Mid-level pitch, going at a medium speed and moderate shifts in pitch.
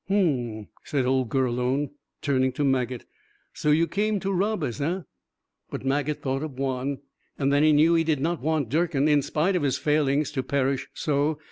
Yes: medium, 145 Hz; average, 190 wpm; average, 3.0 semitones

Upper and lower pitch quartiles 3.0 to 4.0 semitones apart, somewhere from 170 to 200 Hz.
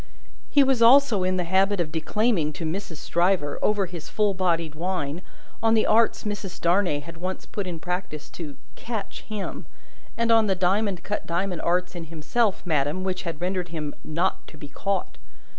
Yes: average, 3.6 semitones; medium, 185 Hz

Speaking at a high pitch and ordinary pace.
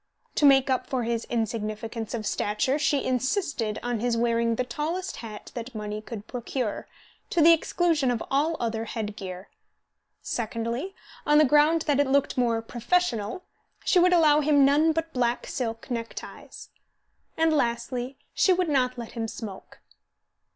Yes: very high, 250 Hz; average, 160 wpm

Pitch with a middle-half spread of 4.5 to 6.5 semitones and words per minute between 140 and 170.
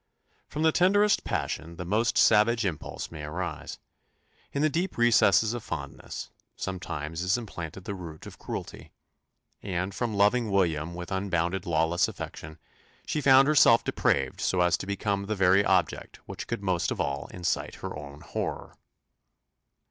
Yes: average, 4.8 semitones; average, 155 wpm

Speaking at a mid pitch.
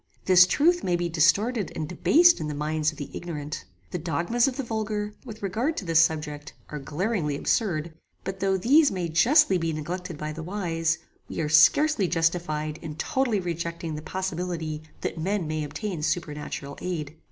Yes: medium, 170 Hz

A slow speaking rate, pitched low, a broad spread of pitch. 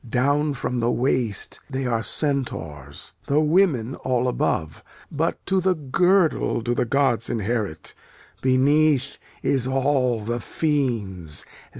No: slow, 120 wpm; low, 130 Hz; average, 4.0 semitones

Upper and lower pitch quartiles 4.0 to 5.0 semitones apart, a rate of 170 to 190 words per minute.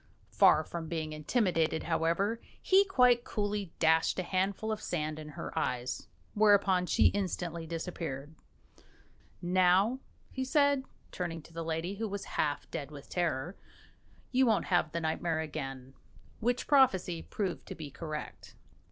No: average, 4.5 semitones; average, 145 wpm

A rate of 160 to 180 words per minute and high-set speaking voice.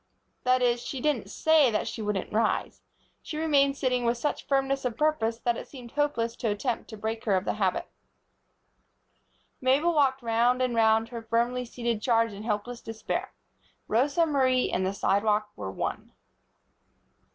Yes: average, 165 wpm; high, 235 Hz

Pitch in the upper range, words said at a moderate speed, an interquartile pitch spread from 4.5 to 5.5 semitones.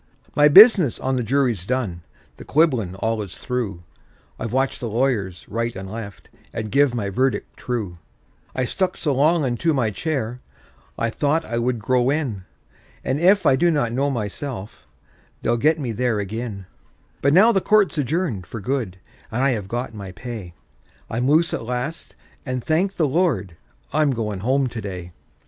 No: low, 125 Hz; average, 170 wpm; average, 5.0 semitones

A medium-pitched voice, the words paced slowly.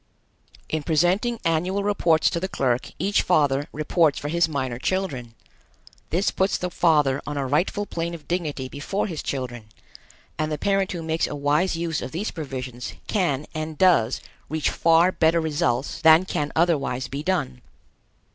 No: medium, 160 Hz; average, 165 wpm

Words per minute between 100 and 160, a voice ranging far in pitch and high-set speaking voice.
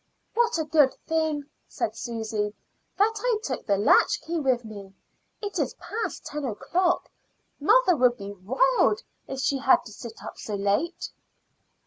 Yes: average, 150 wpm; wide, 8.7 semitones; very high, 275 Hz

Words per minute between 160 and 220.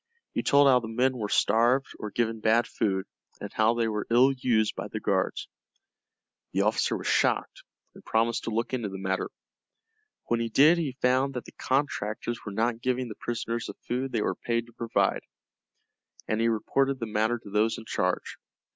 Yes: average, 190 wpm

